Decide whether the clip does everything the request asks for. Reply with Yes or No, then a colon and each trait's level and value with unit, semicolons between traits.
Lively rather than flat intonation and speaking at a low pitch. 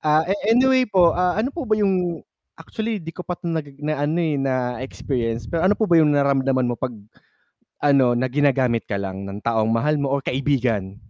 No: wide, 5.8 semitones; medium, 145 Hz